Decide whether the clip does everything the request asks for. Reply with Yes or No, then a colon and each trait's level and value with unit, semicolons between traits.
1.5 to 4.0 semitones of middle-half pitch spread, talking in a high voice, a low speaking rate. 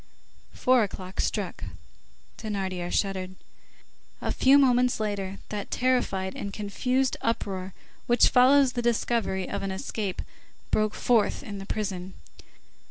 No: average, 4.4 semitones; high, 210 Hz; slow, 120 wpm